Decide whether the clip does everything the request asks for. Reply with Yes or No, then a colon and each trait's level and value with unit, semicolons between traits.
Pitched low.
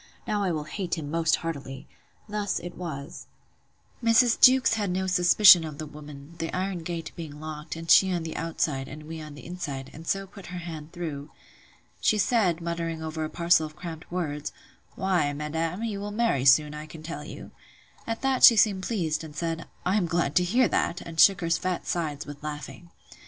No: medium, 165 Hz